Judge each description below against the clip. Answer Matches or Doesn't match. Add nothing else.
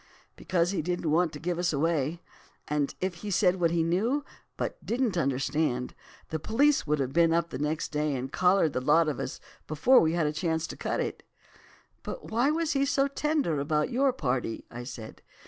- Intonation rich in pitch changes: Doesn't match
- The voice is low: Doesn't match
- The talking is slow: Doesn't match